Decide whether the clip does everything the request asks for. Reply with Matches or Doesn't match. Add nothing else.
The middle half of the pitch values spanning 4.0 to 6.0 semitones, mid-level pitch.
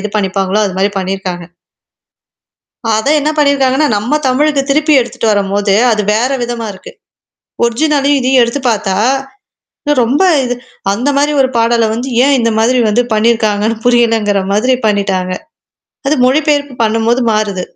Doesn't match